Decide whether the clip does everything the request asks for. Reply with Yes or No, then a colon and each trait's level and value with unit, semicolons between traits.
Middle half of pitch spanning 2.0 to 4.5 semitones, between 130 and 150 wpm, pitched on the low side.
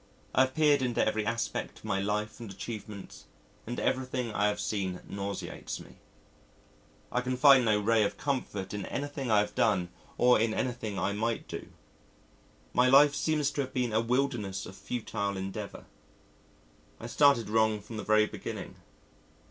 No: average, 3.6 semitones; average, 165 wpm; low, 110 Hz